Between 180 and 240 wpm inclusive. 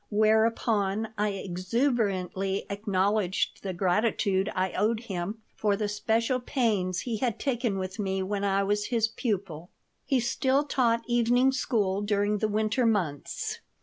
No: average, 140 wpm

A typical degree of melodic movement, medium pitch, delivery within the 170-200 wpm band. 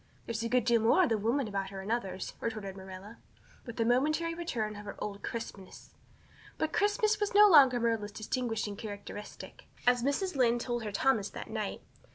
No: average, 4.1 semitones; high, 230 Hz; average, 190 wpm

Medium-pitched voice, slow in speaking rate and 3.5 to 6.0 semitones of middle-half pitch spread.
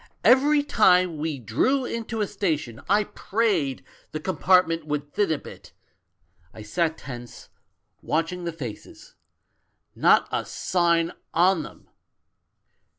Yes: medium, 170 Hz; slow, 125 wpm; average, 5.2 semitones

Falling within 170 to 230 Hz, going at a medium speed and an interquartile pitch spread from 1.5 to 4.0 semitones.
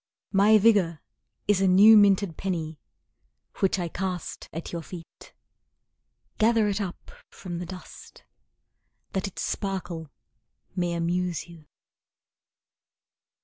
No: medium, 185 Hz; slow, 110 wpm; average, 2.7 semitones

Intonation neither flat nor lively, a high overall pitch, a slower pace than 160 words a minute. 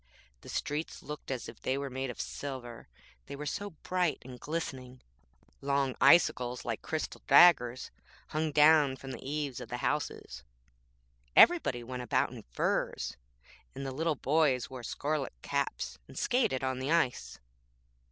No: average, 3.3 semitones; low, 135 Hz; average, 150 wpm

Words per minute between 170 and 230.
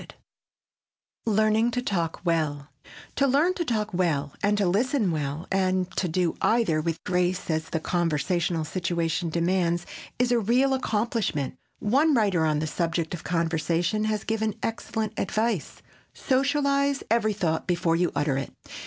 No: average, 150 wpm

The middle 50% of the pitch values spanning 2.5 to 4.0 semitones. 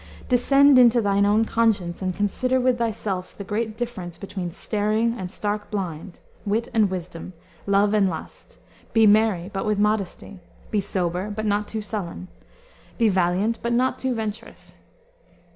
Yes: average, 2.9 semitones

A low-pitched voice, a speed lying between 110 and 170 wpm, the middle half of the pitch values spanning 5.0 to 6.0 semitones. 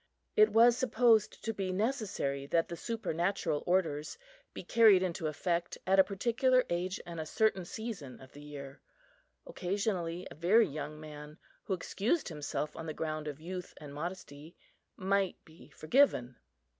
No: medium, 175 Hz; average, 155 wpm; wide, 5.6 semitones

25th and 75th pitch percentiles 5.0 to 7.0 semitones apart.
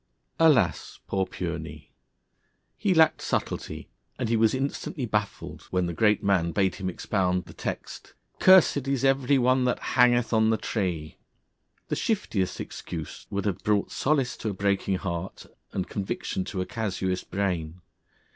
Yes: average, 5.3 semitones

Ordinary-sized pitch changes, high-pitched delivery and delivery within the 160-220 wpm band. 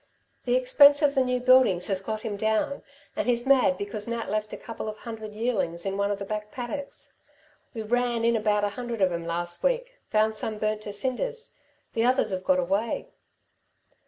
Yes: average, 3.6 semitones; high, 220 Hz; average, 200 wpm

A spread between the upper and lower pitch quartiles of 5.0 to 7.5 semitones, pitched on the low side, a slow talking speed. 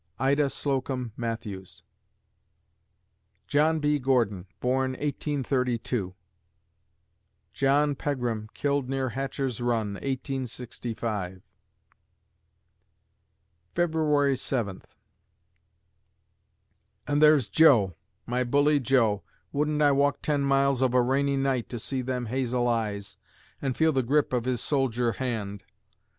No: average, 3.2 semitones; low, 130 Hz; slow, 105 wpm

